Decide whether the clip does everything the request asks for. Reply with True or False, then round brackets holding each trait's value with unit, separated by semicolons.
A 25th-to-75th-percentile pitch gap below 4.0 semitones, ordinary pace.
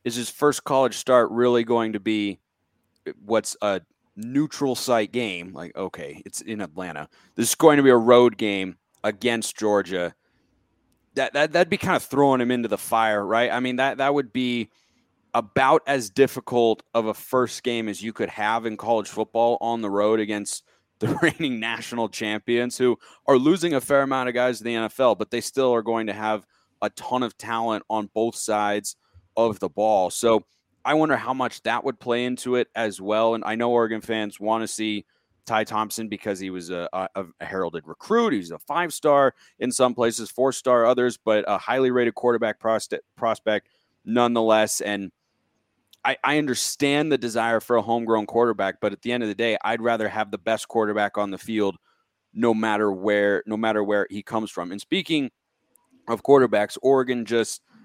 True (2.8 semitones; 190 wpm)